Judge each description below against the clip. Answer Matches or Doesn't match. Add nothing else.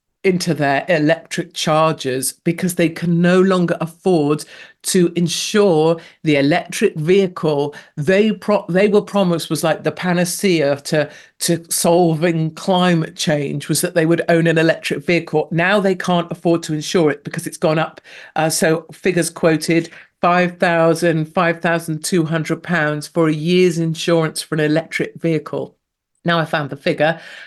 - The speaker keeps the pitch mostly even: Matches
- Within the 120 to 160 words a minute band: Matches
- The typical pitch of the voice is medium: Matches